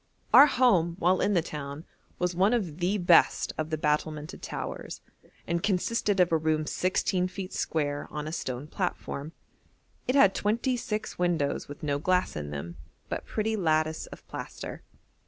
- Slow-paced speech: No, average, 165 wpm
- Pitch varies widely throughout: No, average, 4.2 semitones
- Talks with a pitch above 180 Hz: No, medium, 170 Hz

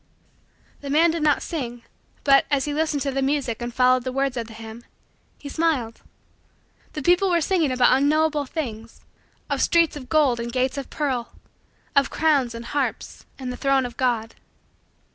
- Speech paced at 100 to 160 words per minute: No, average, 180 wpm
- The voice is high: Yes, very high, 275 Hz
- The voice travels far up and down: No, average, 3.6 semitones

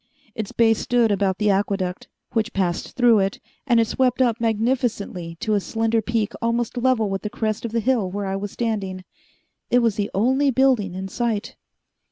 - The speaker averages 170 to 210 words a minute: Yes, average, 190 wpm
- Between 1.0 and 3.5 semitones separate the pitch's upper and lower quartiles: Yes, average, 3.0 semitones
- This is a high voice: Yes, high, 220 Hz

